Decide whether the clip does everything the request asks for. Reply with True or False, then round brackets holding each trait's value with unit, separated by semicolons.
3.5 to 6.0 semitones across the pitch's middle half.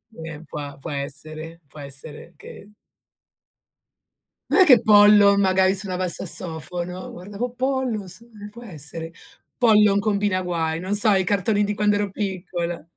True (4.0 semitones)